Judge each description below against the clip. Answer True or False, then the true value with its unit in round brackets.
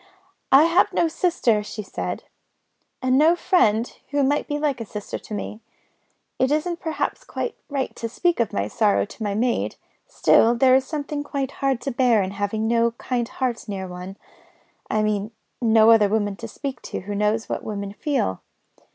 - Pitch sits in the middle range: False (235 Hz)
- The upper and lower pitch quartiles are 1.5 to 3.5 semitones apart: False (5.0 semitones)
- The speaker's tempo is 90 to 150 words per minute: False (180 wpm)